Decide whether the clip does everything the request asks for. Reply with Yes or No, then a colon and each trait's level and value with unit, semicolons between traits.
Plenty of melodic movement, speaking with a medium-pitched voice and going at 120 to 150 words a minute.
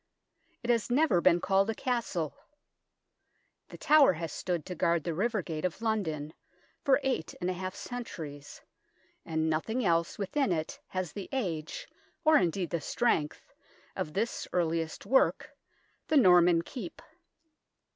Yes: wide, 6.0 semitones; medium, 180 Hz; average, 145 wpm